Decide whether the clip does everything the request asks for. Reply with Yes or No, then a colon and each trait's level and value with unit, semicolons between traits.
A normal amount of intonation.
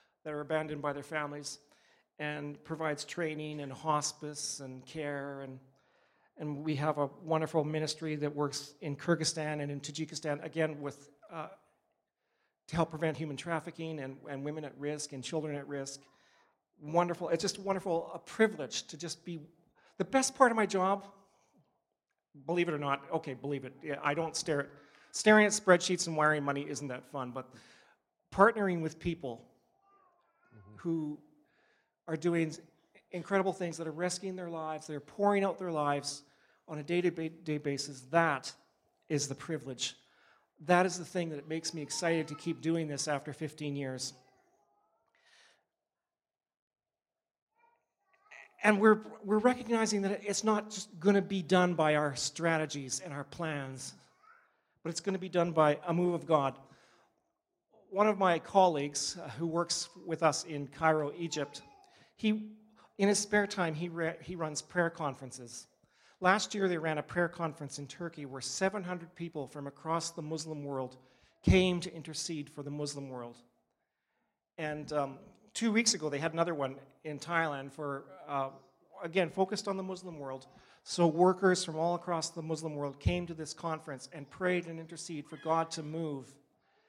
Yes: average, 3.5 semitones